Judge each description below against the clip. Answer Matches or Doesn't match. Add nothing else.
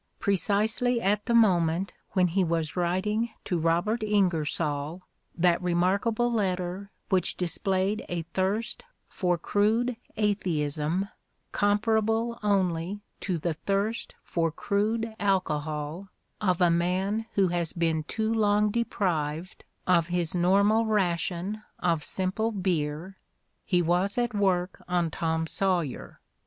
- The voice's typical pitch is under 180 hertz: Doesn't match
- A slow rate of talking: Matches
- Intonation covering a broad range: Doesn't match